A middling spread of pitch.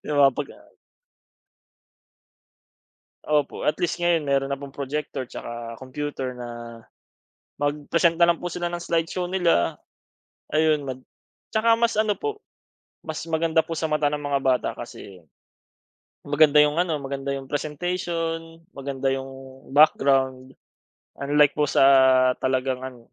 Yes: average, 3.7 semitones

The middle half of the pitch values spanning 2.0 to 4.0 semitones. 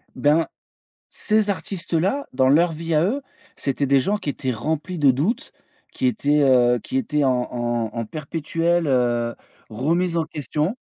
No: average, 4.9 semitones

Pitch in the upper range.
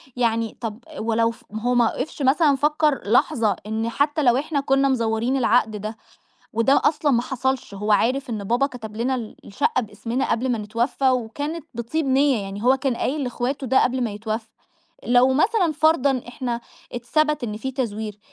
Yes: high, 245 Hz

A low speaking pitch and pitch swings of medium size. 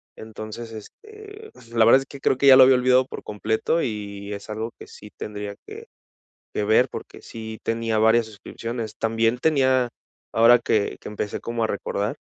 Yes: low, 115 Hz; average, 3.1 semitones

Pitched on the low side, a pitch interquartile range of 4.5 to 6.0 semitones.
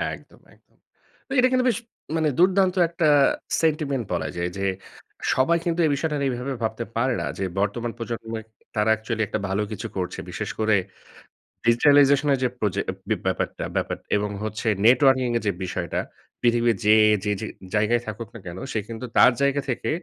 Yes: low, 120 Hz; average, 4.8 semitones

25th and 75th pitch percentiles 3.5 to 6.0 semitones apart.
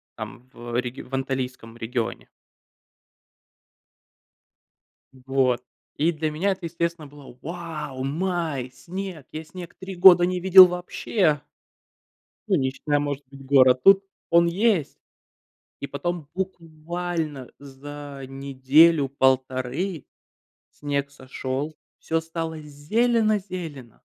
Yes: average, 4.7 semitones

